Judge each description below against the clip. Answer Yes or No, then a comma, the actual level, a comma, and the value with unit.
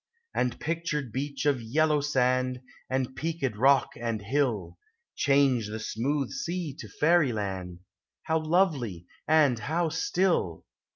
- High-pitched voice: No, low, 135 Hz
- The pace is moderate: No, slow, 120 wpm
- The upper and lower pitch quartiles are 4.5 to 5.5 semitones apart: Yes, average, 4.9 semitones